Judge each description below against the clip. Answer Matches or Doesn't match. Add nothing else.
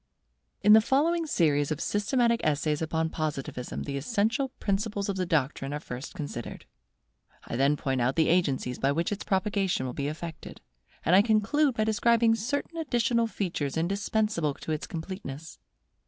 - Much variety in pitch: Matches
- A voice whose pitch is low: Doesn't match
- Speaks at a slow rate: Doesn't match